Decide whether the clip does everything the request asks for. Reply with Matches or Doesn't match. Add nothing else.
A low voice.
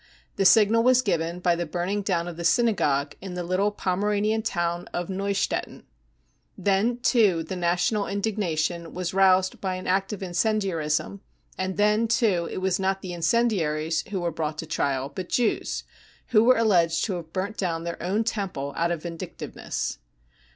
Doesn't match